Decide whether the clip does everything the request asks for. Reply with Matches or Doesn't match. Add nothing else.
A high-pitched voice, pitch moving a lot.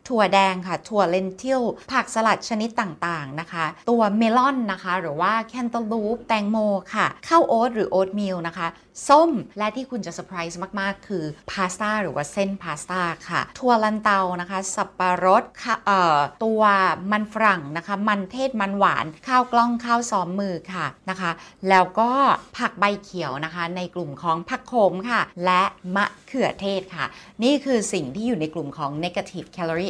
Doesn't match